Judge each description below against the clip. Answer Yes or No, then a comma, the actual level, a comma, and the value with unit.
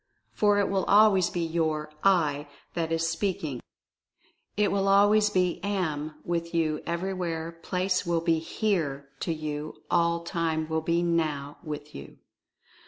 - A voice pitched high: No, medium, 170 Hz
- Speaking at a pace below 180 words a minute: Yes, average, 165 wpm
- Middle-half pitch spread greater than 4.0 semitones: No, average, 2.9 semitones